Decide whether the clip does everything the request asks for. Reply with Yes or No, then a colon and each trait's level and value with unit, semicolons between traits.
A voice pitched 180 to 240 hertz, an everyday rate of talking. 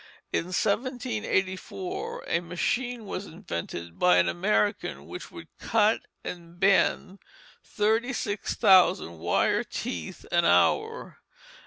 No: high, 190 Hz; slow, 110 wpm